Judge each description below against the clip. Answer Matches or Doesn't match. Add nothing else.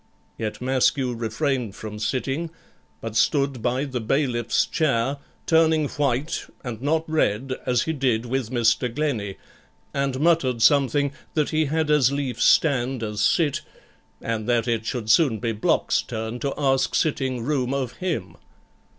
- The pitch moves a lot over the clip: Doesn't match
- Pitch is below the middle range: Matches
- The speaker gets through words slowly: Doesn't match